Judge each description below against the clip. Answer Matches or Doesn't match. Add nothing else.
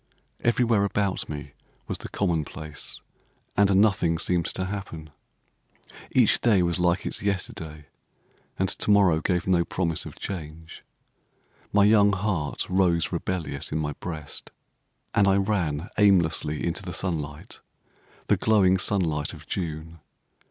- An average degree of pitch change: Matches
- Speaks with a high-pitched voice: Doesn't match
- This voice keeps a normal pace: Doesn't match